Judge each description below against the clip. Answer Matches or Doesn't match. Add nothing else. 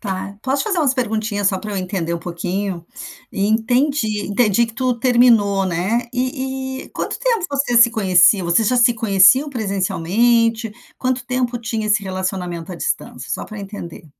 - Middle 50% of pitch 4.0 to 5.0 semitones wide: Matches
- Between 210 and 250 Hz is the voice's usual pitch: Matches